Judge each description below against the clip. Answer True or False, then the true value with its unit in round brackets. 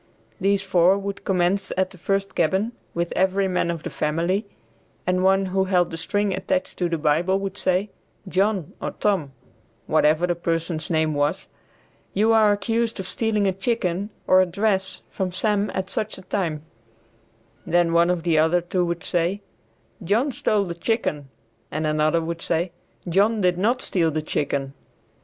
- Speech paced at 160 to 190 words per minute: True (170 wpm)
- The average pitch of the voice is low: False (185 Hz)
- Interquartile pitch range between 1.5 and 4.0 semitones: True (3.0 semitones)